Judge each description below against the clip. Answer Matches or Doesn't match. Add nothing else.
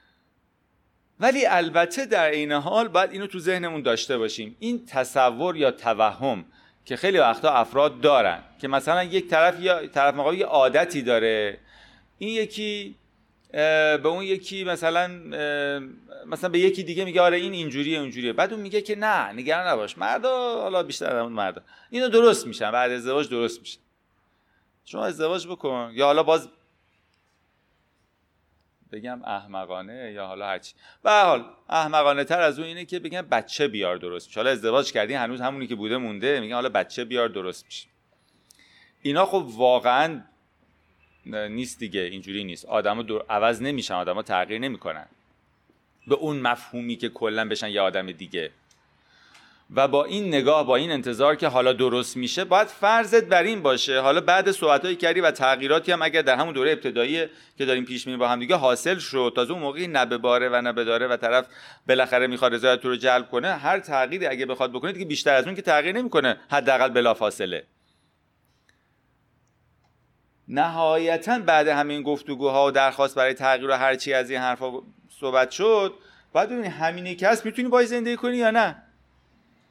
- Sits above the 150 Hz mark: Doesn't match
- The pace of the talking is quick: Matches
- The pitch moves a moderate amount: Doesn't match